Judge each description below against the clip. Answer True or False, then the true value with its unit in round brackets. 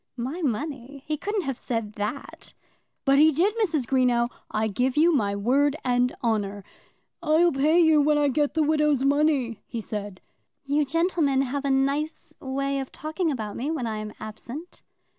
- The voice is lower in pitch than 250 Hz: False (275 Hz)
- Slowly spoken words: False (180 wpm)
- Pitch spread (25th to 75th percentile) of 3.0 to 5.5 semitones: True (4.2 semitones)